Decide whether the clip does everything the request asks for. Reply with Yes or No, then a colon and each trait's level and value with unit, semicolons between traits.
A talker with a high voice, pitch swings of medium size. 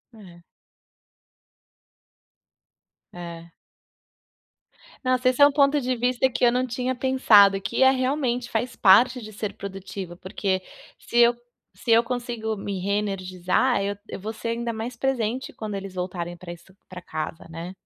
Yes: high, 220 Hz; average, 4.9 semitones